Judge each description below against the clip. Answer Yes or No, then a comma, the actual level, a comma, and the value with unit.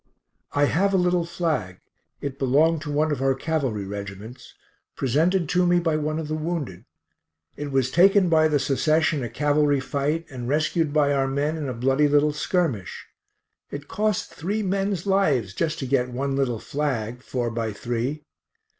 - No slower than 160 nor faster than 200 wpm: Yes, average, 175 wpm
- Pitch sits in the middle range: Yes, medium, 145 Hz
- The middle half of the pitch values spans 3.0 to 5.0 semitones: Yes, average, 3.9 semitones